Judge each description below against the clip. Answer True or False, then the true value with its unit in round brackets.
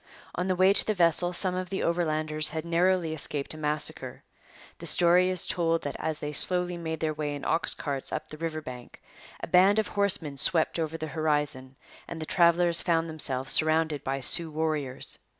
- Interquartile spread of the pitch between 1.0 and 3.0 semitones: True (2.6 semitones)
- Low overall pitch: False (160 Hz)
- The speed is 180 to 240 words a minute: True (195 wpm)